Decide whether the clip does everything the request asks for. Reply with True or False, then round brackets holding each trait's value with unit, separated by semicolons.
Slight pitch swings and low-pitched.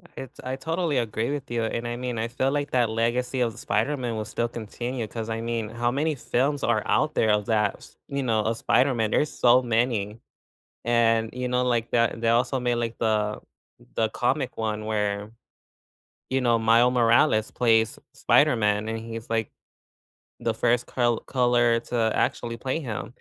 True (1.9 semitones; 115 Hz)